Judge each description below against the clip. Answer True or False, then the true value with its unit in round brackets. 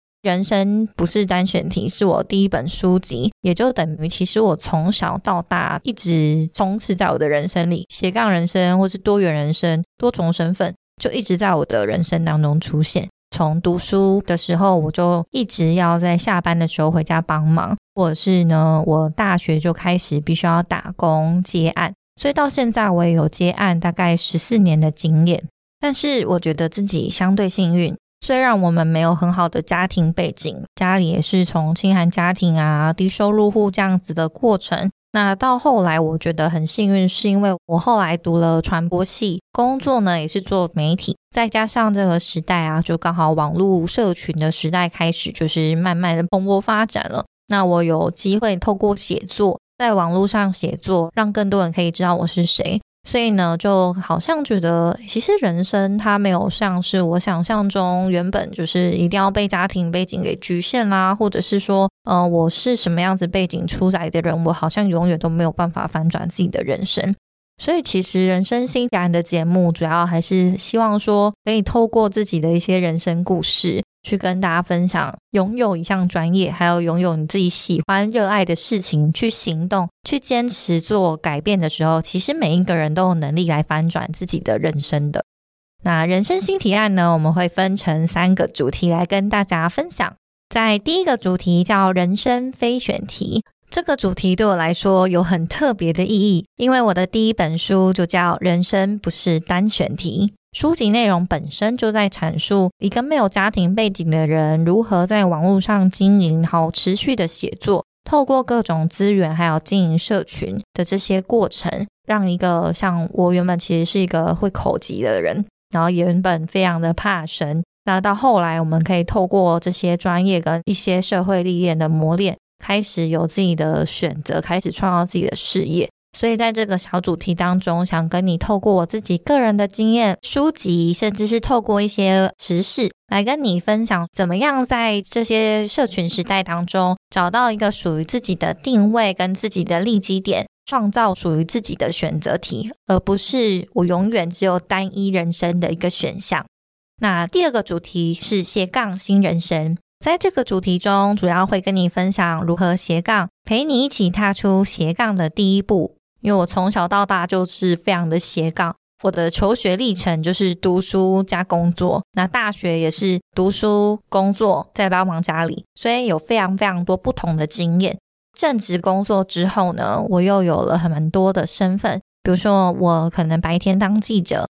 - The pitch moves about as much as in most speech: True (3.1 semitones)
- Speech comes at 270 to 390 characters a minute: True (280 characters per minute)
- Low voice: False (185 Hz)